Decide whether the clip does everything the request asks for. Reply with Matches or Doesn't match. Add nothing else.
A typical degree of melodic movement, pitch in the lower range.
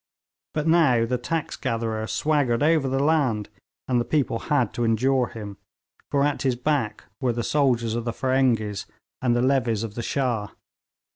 Matches